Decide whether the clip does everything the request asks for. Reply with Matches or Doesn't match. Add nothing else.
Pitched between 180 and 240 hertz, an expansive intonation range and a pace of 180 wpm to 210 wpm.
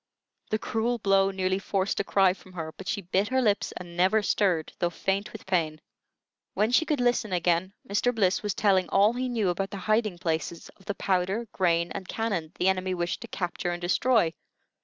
Doesn't match